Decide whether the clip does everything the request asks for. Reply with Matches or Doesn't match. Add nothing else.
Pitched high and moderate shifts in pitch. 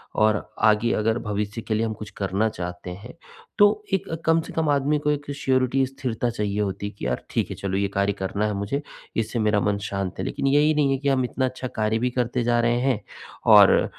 Doesn't match